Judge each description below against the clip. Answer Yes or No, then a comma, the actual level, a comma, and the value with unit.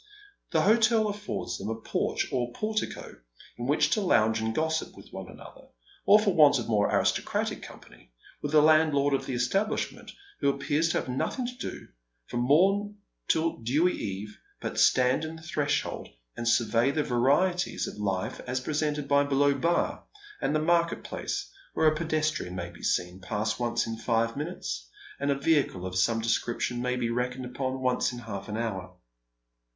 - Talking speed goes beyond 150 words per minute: Yes, average, 180 wpm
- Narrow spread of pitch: No, wide, 5.5 semitones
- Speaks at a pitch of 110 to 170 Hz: Yes, low, 135 Hz